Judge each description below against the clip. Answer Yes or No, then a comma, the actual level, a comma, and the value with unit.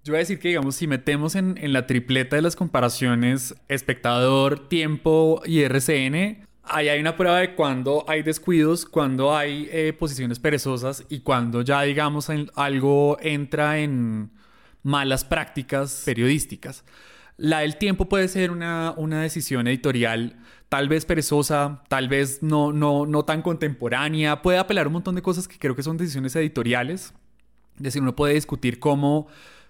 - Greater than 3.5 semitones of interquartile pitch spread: No, average, 2.9 semitones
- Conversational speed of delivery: Yes, average, 160 wpm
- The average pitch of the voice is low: No, medium, 150 Hz